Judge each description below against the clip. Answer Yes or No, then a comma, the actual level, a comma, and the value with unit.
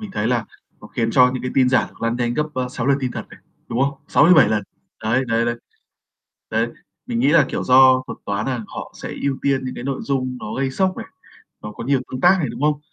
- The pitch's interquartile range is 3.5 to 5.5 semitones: No, average, 2.8 semitones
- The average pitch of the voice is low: Yes, low, 130 Hz